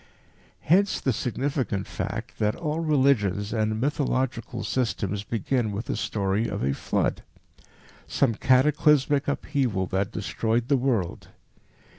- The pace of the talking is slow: Yes, slow, 120 wpm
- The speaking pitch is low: Yes, low, 120 Hz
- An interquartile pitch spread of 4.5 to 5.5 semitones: Yes, average, 5.0 semitones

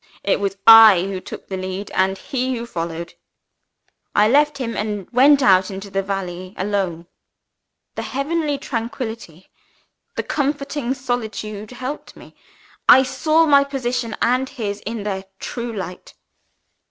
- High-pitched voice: Yes, high, 225 Hz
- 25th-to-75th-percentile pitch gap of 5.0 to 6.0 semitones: Yes, average, 5.3 semitones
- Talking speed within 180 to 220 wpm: No, average, 140 wpm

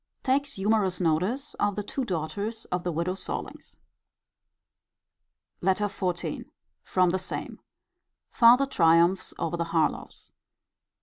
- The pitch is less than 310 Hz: Yes, high, 190 Hz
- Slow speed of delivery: Yes, slow, 115 wpm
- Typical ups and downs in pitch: Yes, average, 4.2 semitones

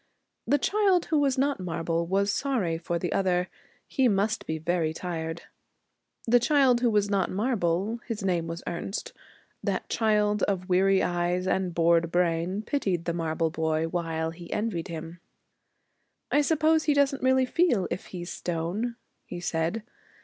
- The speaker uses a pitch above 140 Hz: Yes, medium, 185 Hz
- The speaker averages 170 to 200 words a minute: No, average, 155 wpm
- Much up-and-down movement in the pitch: Yes, wide, 5.7 semitones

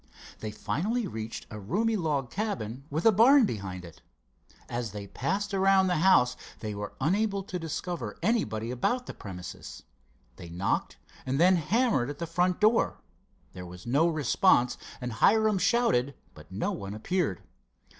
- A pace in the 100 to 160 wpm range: Yes, average, 155 wpm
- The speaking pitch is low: No, medium, 150 Hz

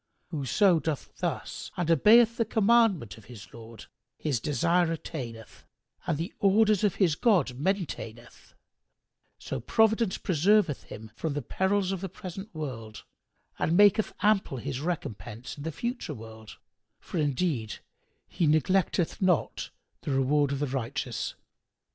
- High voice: No, medium, 160 Hz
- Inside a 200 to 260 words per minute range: No, slow, 135 wpm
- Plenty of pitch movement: Yes, wide, 7.0 semitones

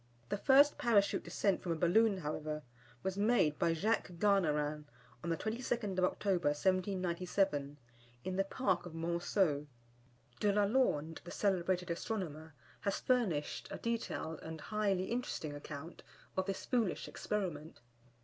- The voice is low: No, medium, 185 Hz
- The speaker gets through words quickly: No, average, 140 wpm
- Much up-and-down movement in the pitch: No, average, 4.4 semitones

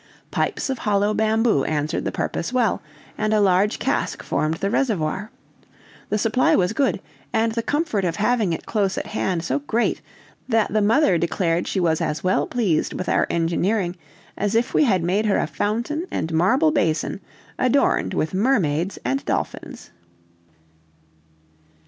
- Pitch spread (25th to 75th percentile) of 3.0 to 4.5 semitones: No, average, 4.9 semitones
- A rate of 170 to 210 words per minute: No, average, 160 wpm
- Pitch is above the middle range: Yes, high, 200 Hz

